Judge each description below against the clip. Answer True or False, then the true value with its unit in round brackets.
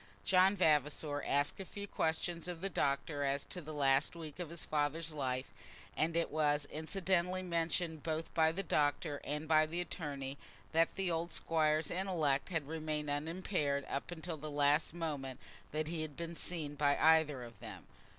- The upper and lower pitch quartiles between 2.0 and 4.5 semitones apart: True (2.6 semitones)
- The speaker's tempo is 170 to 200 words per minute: True (175 wpm)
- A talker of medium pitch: True (155 Hz)